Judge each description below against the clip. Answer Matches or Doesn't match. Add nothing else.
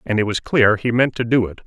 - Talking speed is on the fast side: Matches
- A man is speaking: Matches